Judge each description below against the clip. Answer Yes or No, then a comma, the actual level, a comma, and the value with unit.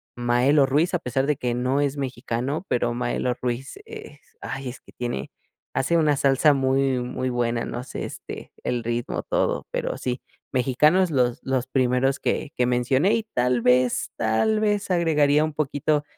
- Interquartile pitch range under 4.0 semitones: Yes, average, 3.2 semitones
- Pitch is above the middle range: No, low, 130 Hz